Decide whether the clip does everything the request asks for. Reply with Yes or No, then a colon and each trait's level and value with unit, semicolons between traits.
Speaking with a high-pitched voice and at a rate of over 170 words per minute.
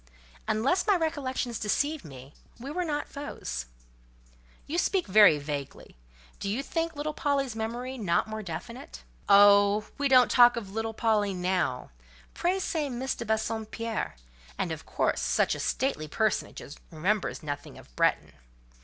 No: high, 220 Hz; average, 145 wpm